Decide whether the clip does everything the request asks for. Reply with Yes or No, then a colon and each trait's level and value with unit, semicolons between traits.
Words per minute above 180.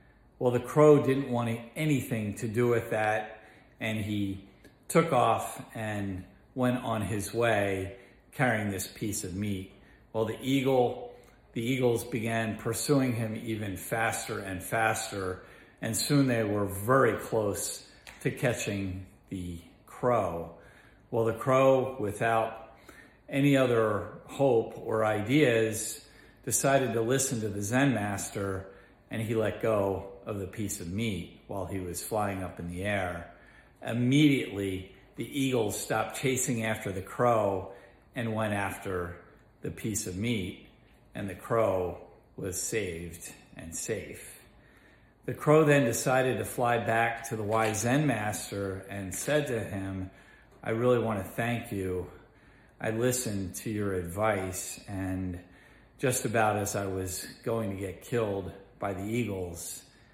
No: average, 140 wpm